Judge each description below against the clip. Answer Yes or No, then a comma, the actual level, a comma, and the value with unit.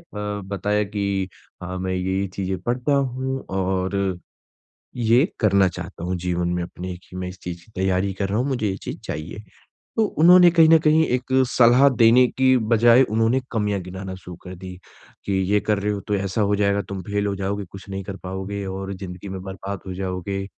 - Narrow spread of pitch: No, average, 3.3 semitones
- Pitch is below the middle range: Yes, low, 100 Hz